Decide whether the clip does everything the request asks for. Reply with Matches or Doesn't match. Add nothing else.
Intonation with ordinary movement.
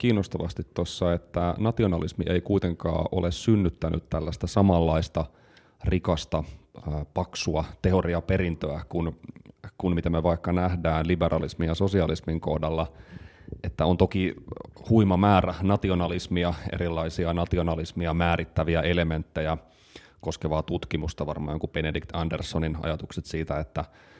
Doesn't match